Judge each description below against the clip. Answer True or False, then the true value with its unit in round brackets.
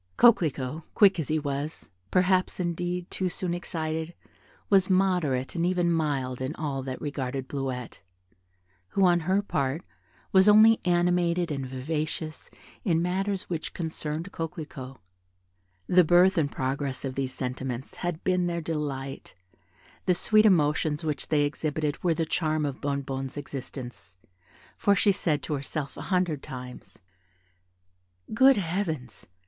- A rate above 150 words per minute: False (135 wpm)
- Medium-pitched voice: True (155 Hz)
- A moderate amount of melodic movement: True (4.6 semitones)